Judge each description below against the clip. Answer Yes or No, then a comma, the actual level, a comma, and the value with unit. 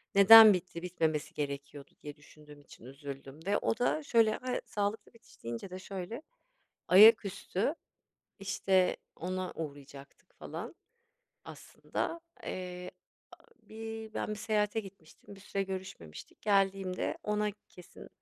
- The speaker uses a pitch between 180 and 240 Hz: Yes, high, 190 Hz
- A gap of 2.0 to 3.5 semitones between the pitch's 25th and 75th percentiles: No, average, 5.3 semitones